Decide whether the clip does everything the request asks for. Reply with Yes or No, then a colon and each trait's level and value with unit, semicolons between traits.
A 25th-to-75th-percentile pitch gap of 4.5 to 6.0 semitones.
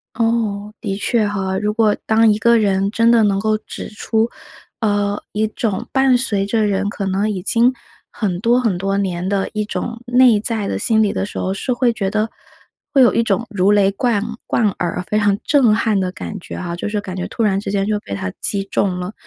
No: narrow, 2.4 semitones